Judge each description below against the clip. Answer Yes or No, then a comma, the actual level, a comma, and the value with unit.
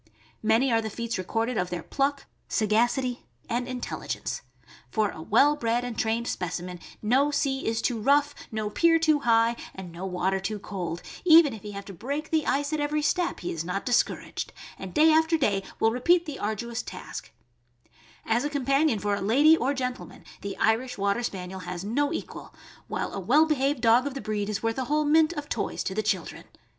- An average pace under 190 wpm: No, average, 200 wpm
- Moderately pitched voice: No, high, 235 Hz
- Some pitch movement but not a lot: No, wide, 5.9 semitones